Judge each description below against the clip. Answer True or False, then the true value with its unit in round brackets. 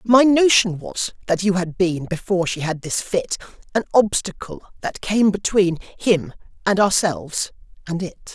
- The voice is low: False (190 Hz)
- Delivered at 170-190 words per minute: False (160 wpm)